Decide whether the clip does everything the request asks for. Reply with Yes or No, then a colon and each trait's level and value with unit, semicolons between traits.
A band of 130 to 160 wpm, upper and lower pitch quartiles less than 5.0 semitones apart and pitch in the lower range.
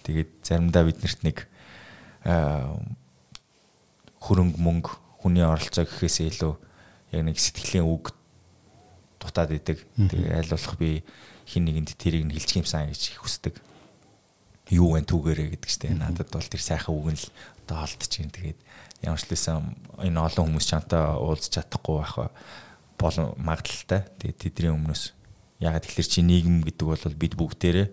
Yes: average, 140 wpm; narrow, 2.4 semitones; very low, 85 Hz